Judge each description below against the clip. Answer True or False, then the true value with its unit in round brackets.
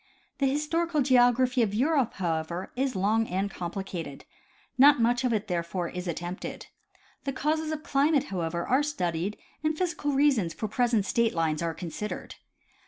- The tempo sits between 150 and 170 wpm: True (160 wpm)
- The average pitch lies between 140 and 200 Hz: False (230 Hz)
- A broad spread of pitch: True (7.6 semitones)